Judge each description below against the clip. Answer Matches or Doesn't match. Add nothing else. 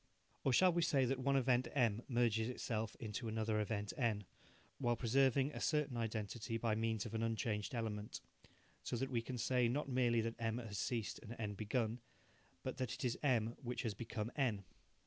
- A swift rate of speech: Doesn't match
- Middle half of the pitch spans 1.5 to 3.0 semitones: Matches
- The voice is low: Matches